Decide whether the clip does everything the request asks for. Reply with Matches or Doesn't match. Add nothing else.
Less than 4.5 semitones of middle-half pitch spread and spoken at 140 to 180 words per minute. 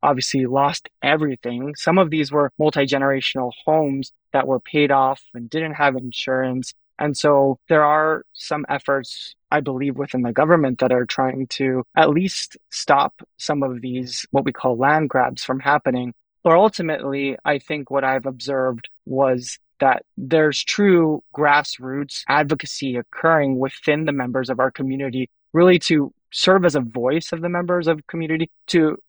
Matches